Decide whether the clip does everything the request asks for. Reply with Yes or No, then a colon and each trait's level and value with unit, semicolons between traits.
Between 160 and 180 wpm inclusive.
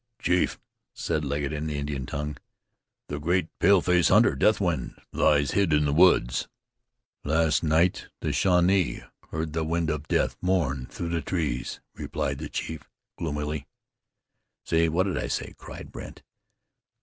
No: average, 145 wpm